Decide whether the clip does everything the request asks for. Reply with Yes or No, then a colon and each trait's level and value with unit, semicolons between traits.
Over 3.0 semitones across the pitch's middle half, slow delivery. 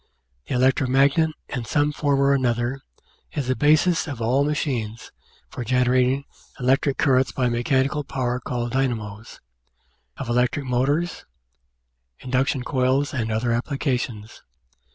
No: narrow, 2.4 semitones; slow, 125 wpm